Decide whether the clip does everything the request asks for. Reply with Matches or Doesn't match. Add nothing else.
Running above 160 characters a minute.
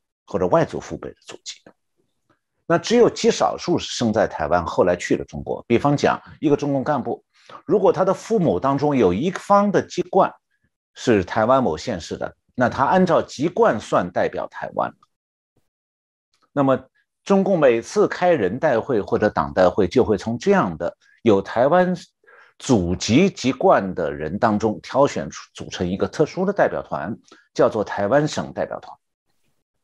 Matches